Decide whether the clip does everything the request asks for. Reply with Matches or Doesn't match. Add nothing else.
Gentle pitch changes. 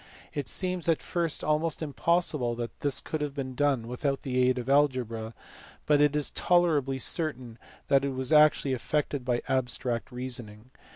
Doesn't match